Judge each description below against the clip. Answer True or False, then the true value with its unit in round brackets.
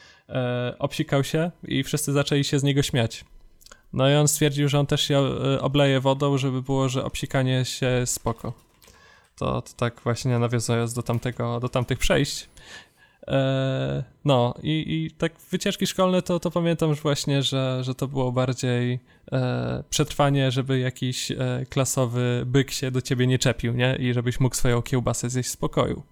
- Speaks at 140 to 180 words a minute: True (160 wpm)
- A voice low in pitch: True (130 Hz)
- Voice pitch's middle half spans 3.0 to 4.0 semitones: False (2.5 semitones)